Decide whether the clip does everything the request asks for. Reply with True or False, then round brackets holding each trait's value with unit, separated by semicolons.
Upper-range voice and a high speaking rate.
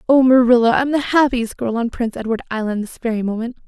True (240 Hz; 210 wpm)